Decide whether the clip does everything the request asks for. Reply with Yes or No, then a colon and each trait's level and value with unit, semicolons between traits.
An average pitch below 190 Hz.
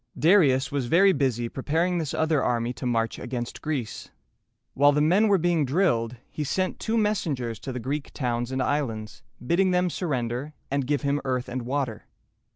Yes: medium, 140 Hz